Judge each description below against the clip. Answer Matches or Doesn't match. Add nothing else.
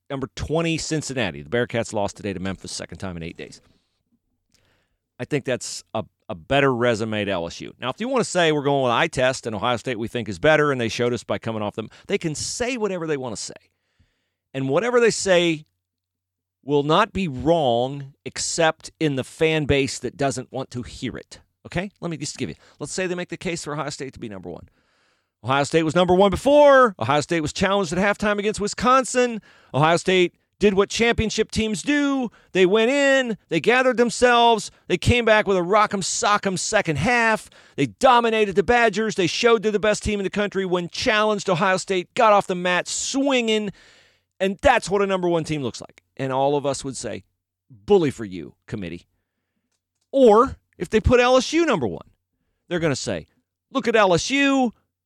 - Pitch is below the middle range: Doesn't match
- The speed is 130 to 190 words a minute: Doesn't match